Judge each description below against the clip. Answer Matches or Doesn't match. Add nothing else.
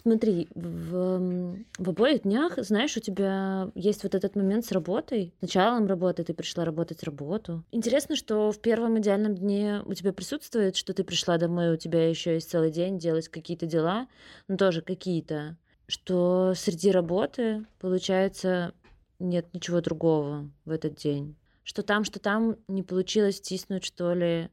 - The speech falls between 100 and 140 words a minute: Doesn't match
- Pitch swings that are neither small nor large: Matches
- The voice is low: Doesn't match